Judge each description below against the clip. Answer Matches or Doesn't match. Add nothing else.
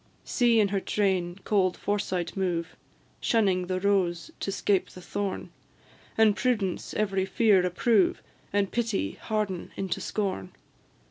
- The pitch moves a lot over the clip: Doesn't match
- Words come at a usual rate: Doesn't match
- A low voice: Doesn't match